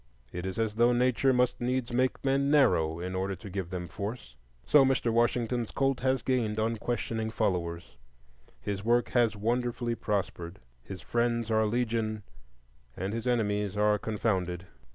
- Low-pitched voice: Yes, low, 110 Hz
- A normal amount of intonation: Yes, average, 3.6 semitones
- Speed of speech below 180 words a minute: Yes, average, 155 wpm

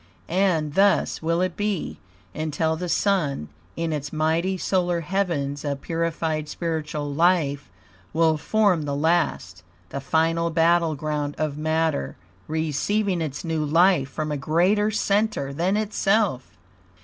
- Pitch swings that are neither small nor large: Yes, average, 3.2 semitones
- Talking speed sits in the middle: No, slow, 130 wpm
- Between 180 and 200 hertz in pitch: No, medium, 160 Hz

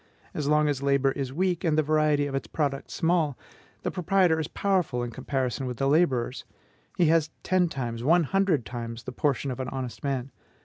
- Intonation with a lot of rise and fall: No, average, 3.8 semitones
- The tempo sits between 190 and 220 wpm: Yes, average, 195 wpm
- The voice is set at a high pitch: No, medium, 140 Hz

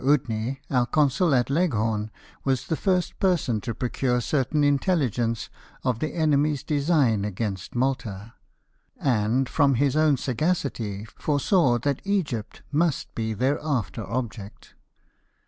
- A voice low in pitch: Yes, low, 130 Hz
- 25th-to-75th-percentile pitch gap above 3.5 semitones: Yes, average, 4.6 semitones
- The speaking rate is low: Yes, slow, 125 wpm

